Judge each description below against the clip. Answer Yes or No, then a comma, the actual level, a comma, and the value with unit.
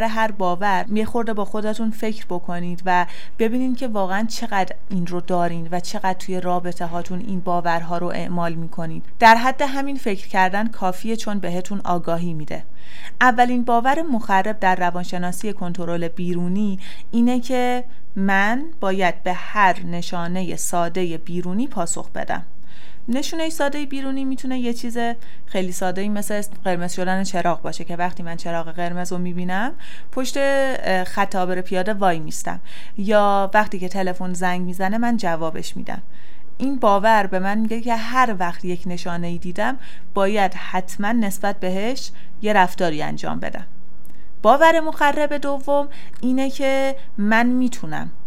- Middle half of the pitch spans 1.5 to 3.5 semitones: No, average, 4.7 semitones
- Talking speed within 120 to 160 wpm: Yes, average, 145 wpm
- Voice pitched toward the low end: No, high, 195 Hz